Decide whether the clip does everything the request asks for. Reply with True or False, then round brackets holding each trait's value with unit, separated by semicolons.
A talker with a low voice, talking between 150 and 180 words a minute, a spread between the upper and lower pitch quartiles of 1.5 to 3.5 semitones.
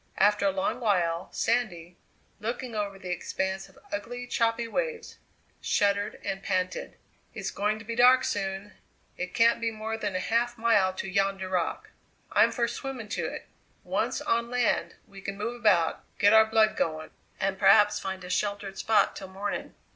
False (205 Hz; 170 wpm; 3.2 semitones)